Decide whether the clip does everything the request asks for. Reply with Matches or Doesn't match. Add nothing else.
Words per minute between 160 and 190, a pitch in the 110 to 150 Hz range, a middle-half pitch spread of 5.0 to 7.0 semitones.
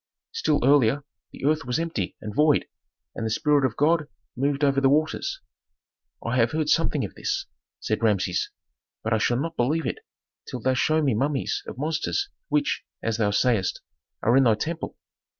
Matches